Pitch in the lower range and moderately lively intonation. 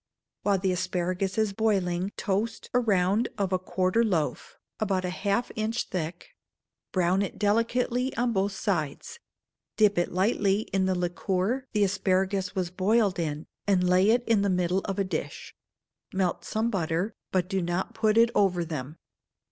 No: high, 195 Hz; average, 3.0 semitones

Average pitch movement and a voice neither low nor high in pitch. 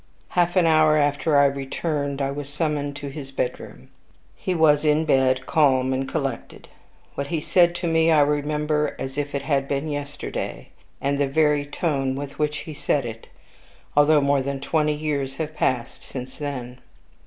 No: narrow, 1.9 semitones; medium, 145 Hz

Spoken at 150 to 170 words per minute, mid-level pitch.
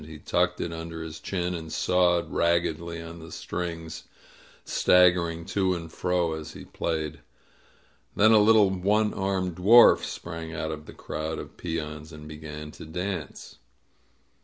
No: average, 160 wpm; very low, 85 Hz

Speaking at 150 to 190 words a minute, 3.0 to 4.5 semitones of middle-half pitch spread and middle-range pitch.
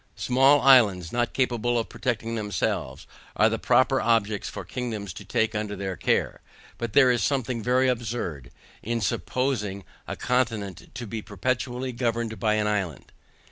No: average, 155 wpm; average, 3.3 semitones; low, 115 Hz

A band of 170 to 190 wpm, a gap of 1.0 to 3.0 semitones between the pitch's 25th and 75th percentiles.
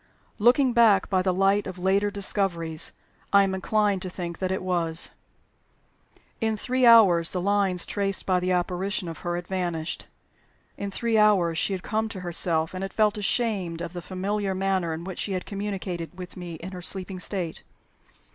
Yes: average, 185 wpm; narrow, 2.4 semitones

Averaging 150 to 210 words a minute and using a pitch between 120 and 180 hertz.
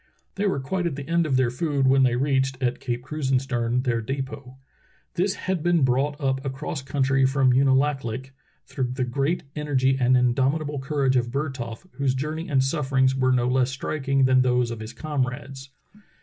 Yes: average, 180 wpm; low, 135 Hz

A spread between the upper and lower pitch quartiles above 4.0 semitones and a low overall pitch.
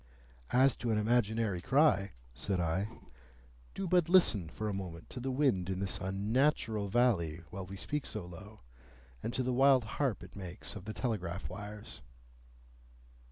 Yes: average, 4.9 semitones; low, 105 Hz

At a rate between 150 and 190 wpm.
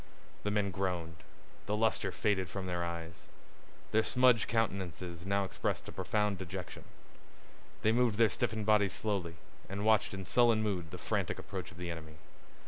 Yes: average, 160 wpm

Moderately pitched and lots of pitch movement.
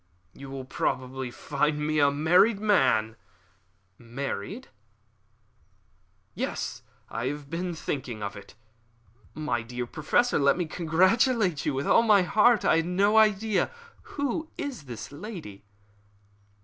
Yes: medium, 155 Hz; wide, 7.6 semitones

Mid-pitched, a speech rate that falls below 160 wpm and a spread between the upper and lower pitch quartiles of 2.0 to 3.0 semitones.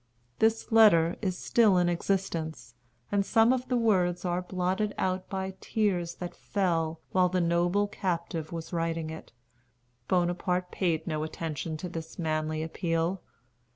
Yes: medium, 175 Hz; average, 145 wpm; average, 2.7 semitones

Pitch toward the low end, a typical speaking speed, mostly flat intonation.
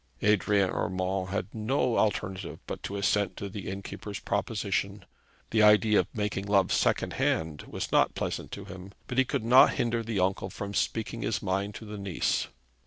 Yes: low, 100 Hz; average, 175 wpm; narrow, 2.2 semitones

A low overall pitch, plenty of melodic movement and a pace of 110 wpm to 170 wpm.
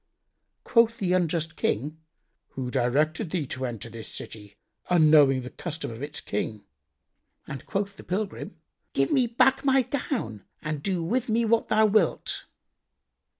No: medium, 160 Hz; wide, 8.8 semitones; average, 150 wpm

